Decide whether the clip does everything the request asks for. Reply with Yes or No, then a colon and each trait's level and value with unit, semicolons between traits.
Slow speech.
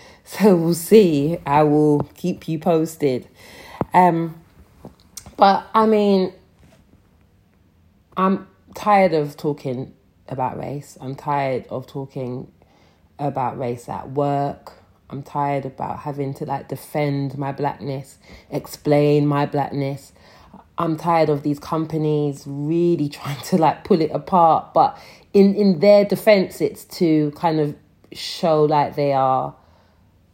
Yes: slow, 125 wpm